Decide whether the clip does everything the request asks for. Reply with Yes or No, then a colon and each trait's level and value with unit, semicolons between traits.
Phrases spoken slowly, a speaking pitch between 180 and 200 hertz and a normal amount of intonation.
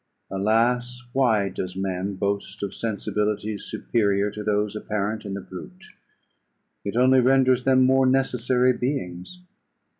No: slow, 125 wpm; low, 110 Hz; average, 4.2 semitones